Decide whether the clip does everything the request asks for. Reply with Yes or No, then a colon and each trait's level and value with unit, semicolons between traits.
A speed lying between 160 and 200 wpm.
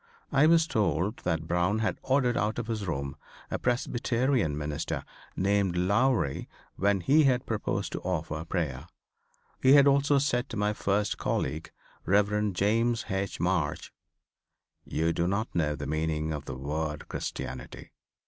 No: average, 150 wpm